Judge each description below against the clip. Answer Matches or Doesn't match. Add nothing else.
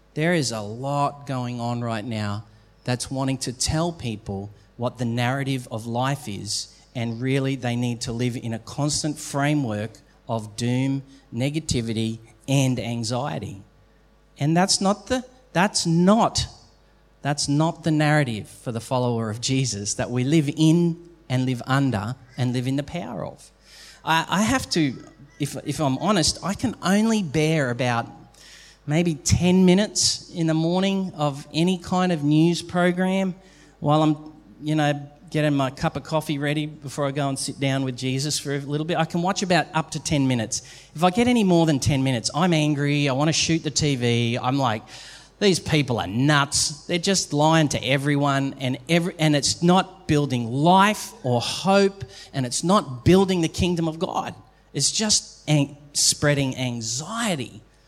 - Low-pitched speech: Doesn't match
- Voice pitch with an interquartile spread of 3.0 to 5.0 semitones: Matches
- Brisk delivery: Doesn't match